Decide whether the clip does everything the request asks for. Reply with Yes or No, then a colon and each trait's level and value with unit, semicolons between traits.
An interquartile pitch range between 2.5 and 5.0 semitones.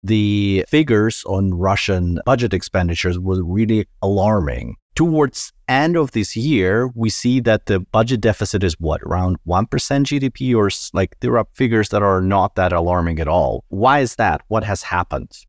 Yes: average, 4.2 semitones